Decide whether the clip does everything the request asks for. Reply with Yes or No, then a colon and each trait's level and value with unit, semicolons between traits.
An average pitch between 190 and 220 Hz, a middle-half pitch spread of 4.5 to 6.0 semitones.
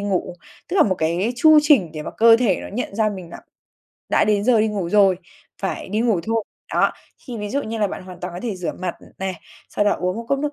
No: high, 205 Hz; average, 3.8 semitones